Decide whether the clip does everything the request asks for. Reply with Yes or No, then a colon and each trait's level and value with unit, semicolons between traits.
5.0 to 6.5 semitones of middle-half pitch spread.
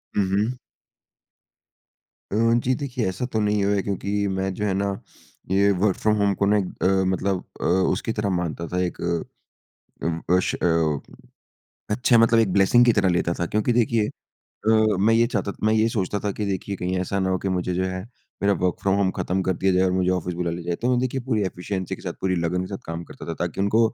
No: narrow, 2.6 semitones